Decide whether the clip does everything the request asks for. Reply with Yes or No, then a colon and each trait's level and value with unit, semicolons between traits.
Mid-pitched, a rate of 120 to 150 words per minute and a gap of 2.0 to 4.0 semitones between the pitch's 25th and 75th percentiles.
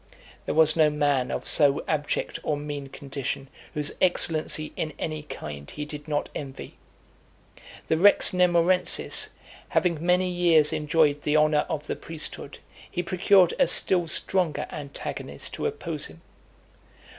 Yes: medium, 155 Hz; average, 140 wpm; average, 2.9 semitones